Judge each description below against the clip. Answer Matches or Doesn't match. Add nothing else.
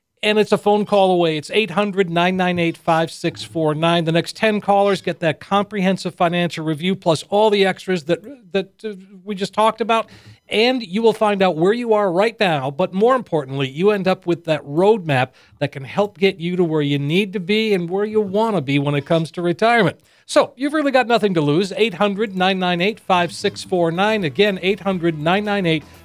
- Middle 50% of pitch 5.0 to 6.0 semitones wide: Doesn't match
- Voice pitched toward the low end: Doesn't match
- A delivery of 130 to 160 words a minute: Doesn't match